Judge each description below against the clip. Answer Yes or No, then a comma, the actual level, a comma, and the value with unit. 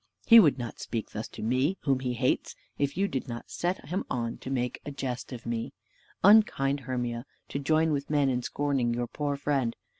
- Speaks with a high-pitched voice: No, low, 135 Hz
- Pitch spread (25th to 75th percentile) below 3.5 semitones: Yes, average, 3.0 semitones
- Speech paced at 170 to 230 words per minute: Yes, fast, 205 wpm